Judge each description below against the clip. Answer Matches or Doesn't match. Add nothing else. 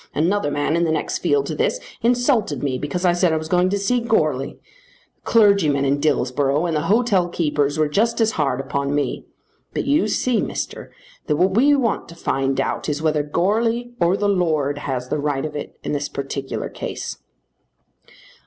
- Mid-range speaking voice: Matches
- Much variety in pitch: Matches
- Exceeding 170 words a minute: Matches